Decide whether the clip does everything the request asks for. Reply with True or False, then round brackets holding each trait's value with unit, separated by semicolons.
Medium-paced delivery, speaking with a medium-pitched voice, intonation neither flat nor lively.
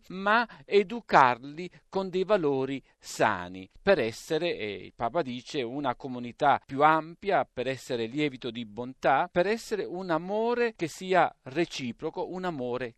False (140 wpm; 155 Hz; 6.8 semitones)